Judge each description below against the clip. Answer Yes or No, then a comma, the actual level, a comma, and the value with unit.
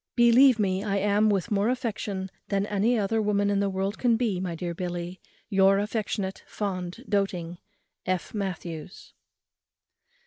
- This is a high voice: Yes, high, 200 Hz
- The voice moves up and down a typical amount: No, narrow, 2.3 semitones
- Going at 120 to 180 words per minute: Yes, average, 145 wpm